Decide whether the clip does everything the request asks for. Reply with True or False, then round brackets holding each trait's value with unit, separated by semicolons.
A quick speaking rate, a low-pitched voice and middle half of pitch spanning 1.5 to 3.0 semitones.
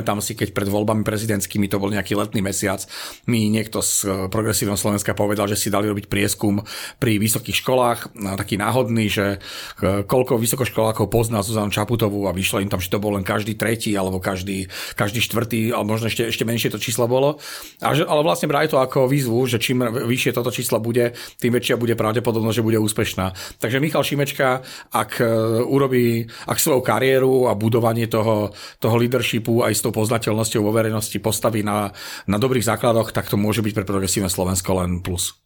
True (185 wpm; 110 Hz; 2.6 semitones)